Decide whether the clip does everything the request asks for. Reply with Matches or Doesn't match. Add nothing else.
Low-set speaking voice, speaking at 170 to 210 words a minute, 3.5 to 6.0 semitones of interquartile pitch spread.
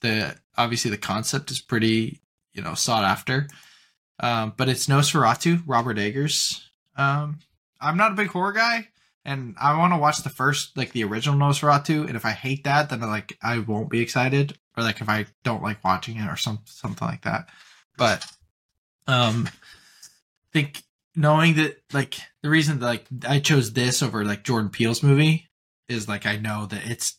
Matches